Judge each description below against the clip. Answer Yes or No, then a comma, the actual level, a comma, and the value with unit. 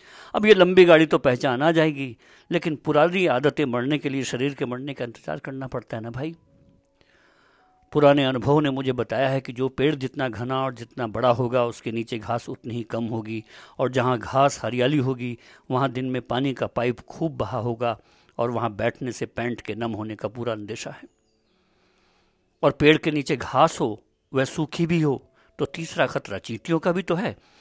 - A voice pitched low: Yes, low, 130 Hz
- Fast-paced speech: Yes, fast, 195 wpm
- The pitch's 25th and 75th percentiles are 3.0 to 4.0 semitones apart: Yes, average, 3.7 semitones